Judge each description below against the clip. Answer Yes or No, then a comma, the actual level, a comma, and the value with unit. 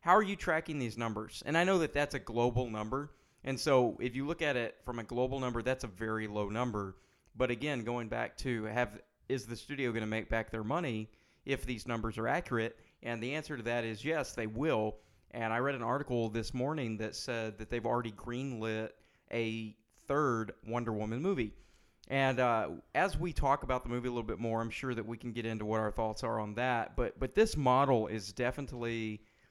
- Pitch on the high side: No, low, 120 Hz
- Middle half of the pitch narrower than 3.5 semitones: Yes, average, 3.0 semitones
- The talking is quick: Yes, fast, 220 wpm